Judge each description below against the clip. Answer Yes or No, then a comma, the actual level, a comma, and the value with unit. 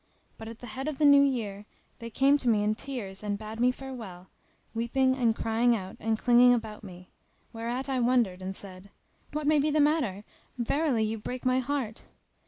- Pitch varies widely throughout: No, average, 3.8 semitones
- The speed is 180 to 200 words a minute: Yes, average, 195 wpm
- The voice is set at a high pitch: Yes, high, 235 Hz